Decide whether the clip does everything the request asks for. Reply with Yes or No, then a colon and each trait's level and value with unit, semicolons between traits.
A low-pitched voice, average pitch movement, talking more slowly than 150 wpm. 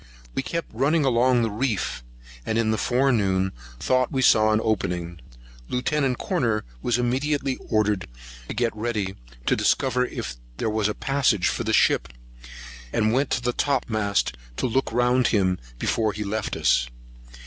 No: low, 115 Hz; average, 3.4 semitones; average, 160 wpm